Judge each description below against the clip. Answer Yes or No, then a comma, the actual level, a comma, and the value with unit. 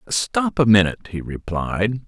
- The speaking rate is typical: Yes, average, 145 wpm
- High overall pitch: No, low, 115 Hz